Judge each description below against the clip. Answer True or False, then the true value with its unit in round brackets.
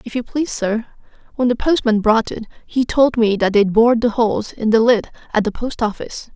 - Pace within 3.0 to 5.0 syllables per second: False (5.7 syllables/s)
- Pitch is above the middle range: True (230 Hz)